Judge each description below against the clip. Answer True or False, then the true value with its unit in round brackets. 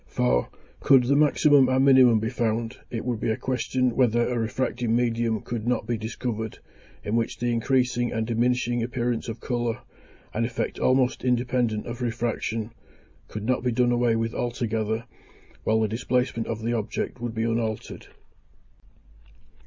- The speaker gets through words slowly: False (160 wpm)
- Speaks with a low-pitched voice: True (120 Hz)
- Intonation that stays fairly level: True (1.7 semitones)